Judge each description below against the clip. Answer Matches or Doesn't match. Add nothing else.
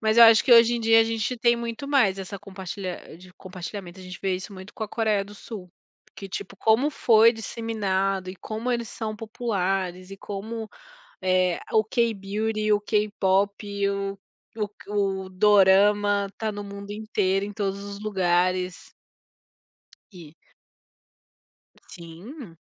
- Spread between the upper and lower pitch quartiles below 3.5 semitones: Matches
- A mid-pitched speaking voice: Doesn't match